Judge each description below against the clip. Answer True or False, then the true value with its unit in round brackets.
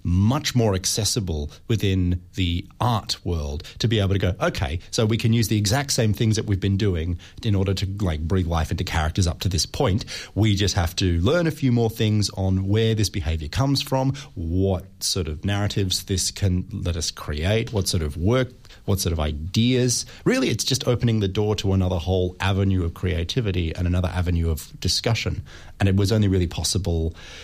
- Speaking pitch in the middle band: False (95 Hz)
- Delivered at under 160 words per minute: False (200 wpm)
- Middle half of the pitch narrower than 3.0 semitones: False (3.8 semitones)